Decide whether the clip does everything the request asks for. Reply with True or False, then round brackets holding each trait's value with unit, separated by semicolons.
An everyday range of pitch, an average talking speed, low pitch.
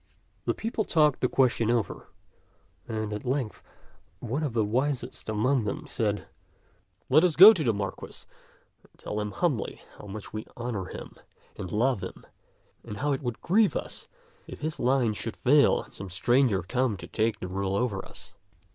True (4.8 semitones; 180 wpm; 120 Hz)